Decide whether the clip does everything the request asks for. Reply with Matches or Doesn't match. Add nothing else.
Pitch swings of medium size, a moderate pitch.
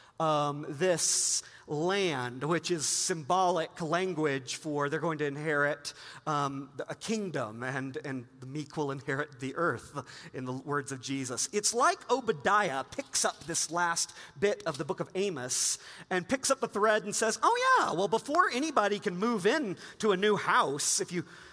Doesn't match